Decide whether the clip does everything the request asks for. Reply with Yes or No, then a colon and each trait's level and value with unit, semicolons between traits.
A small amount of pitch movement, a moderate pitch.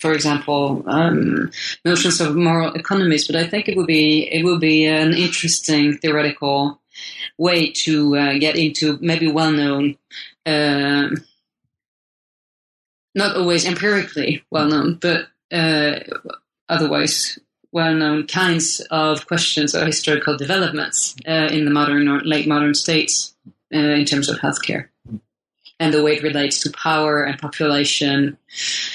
Yes: narrow, 1.9 semitones; medium, 155 Hz